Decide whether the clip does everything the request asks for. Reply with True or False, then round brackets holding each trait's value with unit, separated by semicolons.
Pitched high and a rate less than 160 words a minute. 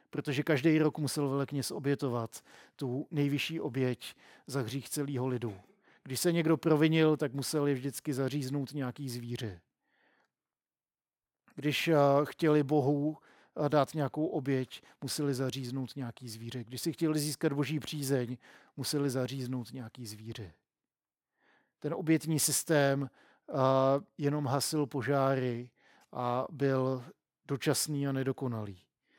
False (140 Hz; 115 wpm)